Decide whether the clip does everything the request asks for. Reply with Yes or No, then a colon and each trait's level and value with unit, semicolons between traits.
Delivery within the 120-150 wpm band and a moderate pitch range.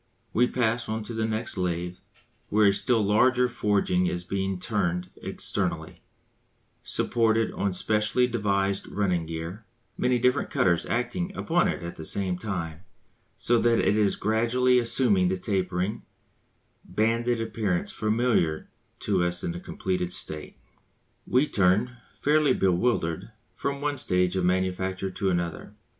Yes: average, 140 wpm; average, 4.4 semitones